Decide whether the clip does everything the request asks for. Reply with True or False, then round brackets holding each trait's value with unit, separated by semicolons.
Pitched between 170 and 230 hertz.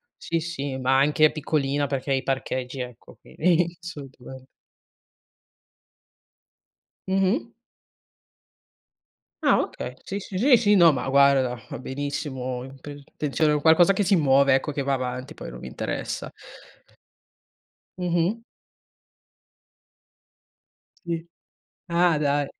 False (145 Hz)